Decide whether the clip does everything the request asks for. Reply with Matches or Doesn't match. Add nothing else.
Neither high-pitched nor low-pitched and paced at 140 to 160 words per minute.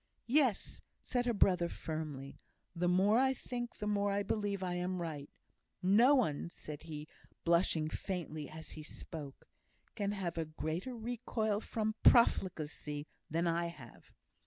Matches